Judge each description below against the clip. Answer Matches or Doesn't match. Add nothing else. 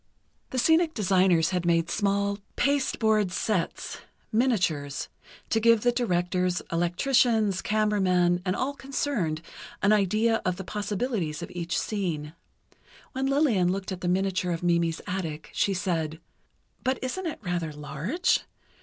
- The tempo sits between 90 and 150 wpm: Matches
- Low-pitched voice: Doesn't match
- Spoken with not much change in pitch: Doesn't match